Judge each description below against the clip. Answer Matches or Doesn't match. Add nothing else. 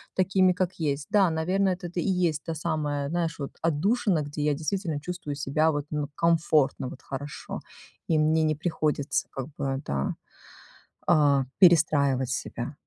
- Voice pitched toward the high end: Doesn't match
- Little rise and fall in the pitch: Doesn't match